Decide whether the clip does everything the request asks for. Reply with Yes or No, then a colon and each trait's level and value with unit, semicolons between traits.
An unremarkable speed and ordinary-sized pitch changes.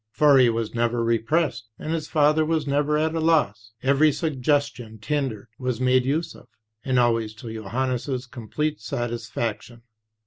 Yes: average, 150 wpm; average, 4.4 semitones